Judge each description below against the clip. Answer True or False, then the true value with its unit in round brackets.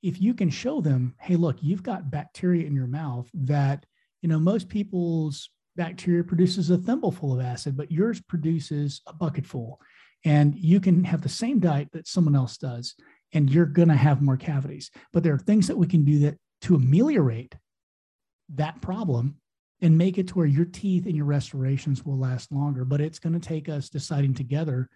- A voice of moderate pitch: True (155 Hz)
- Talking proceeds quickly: False (195 wpm)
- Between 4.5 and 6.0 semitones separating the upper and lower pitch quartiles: False (3.7 semitones)